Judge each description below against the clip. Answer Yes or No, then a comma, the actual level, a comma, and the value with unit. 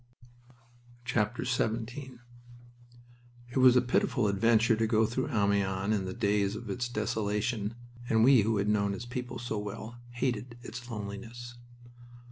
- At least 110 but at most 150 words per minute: Yes, slow, 135 wpm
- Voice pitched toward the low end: Yes, low, 110 Hz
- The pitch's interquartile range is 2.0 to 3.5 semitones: Yes, average, 2.8 semitones